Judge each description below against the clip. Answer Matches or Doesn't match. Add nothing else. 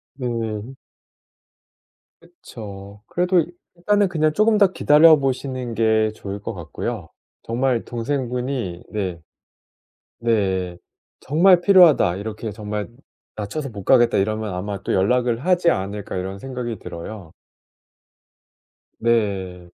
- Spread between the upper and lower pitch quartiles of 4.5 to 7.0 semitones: Matches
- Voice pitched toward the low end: Matches